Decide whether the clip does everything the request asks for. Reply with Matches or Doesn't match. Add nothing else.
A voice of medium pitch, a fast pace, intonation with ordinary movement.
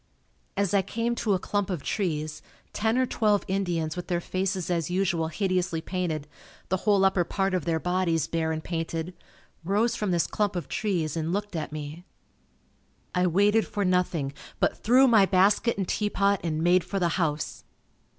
Doesn't match